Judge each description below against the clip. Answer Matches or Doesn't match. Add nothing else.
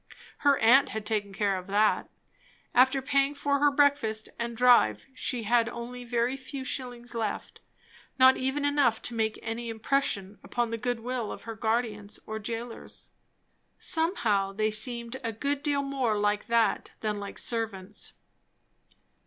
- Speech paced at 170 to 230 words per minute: Doesn't match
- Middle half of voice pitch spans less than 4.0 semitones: Matches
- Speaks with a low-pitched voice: Doesn't match